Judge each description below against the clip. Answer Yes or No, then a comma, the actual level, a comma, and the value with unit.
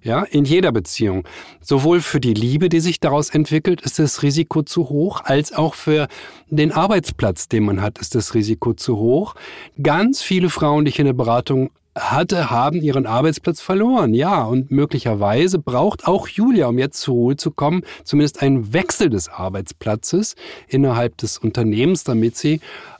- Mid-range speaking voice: Yes, medium, 145 Hz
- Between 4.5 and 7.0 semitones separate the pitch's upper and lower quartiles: Yes, wide, 5.5 semitones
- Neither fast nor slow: Yes, average, 170 wpm